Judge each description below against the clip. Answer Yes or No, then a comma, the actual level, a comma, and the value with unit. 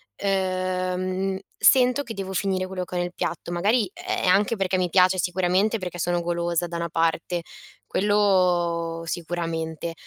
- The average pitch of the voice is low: No, medium, 180 Hz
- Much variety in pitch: No, narrow, 1.9 semitones